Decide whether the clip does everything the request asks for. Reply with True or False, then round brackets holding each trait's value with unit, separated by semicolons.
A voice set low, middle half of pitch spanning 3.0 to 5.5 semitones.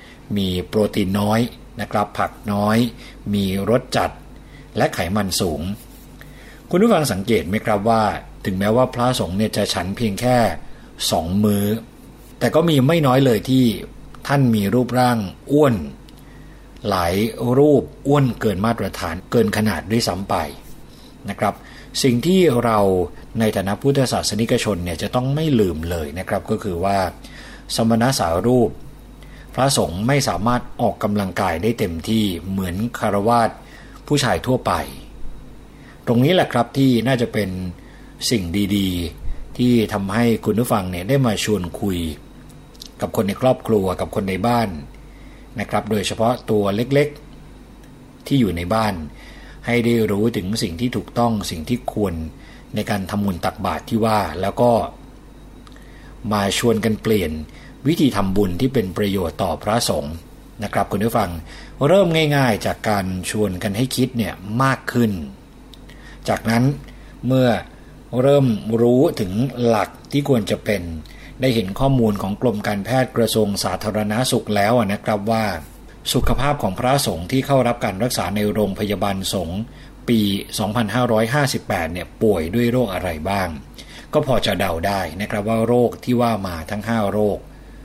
True (110 Hz; 3.7 semitones)